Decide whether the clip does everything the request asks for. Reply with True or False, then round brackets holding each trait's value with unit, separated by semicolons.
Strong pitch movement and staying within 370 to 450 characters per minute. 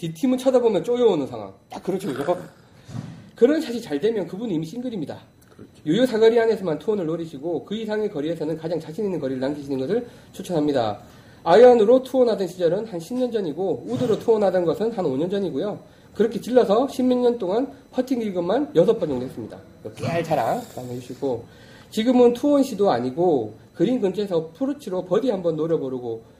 True (7.3 semitones; 385 characters per minute)